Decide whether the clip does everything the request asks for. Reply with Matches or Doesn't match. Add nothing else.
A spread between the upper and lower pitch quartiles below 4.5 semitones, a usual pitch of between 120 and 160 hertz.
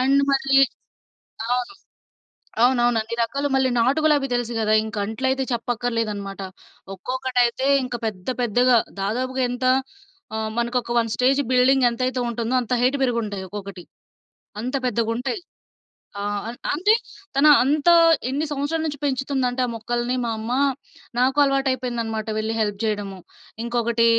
Doesn't match